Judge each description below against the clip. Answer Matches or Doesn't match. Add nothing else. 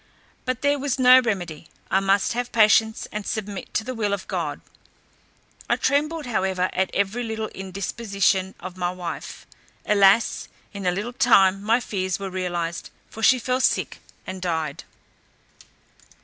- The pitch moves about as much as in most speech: Matches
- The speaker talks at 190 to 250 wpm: Doesn't match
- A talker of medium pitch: Doesn't match